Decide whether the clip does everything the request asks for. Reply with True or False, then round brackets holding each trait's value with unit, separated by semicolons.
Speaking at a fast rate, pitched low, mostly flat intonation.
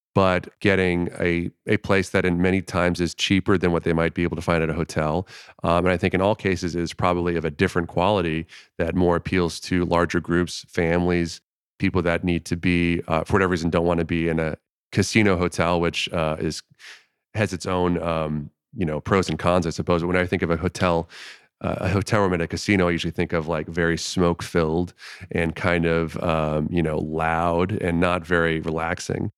True (215 wpm; 85 Hz; 1.6 semitones)